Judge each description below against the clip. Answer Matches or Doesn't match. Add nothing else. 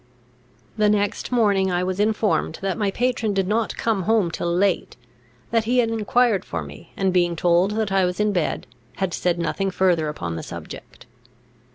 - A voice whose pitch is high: Matches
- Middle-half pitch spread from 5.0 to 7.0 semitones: Doesn't match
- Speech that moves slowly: Doesn't match